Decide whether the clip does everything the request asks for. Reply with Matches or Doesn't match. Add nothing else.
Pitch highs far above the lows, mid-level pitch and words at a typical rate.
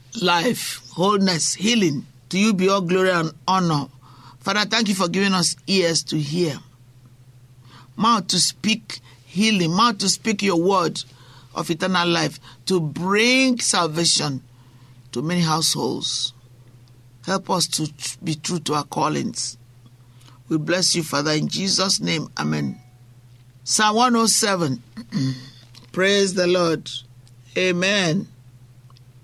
Doesn't match